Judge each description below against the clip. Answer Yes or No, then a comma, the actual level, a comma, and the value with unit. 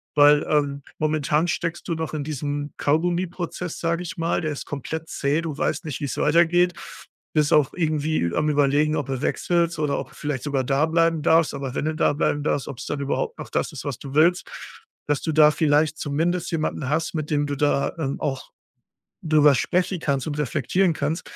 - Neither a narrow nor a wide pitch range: No, narrow, 2.3 semitones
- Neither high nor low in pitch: Yes, medium, 150 Hz